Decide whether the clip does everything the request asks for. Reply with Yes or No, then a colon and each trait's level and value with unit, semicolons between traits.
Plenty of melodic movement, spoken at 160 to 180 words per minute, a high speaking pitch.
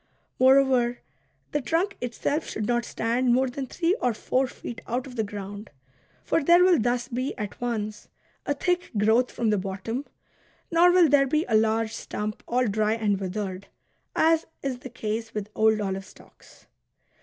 No: average, 4.1 semitones; average, 170 wpm; high, 240 Hz